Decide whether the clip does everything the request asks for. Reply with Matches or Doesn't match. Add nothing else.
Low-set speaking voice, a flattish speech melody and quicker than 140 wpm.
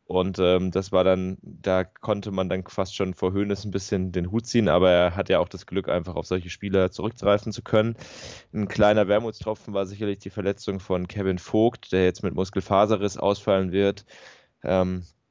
Matches